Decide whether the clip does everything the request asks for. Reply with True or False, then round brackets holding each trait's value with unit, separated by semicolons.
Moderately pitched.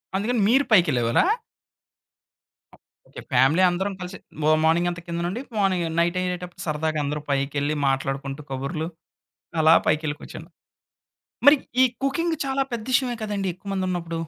True (170 Hz)